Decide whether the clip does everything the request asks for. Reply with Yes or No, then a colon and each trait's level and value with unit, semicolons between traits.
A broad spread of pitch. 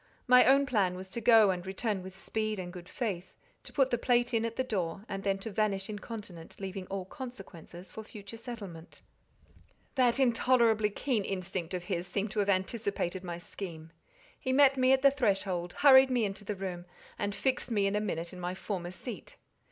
No: average, 4.3 semitones